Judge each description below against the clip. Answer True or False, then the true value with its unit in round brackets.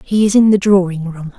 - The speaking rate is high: True (260 wpm)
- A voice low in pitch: False (190 Hz)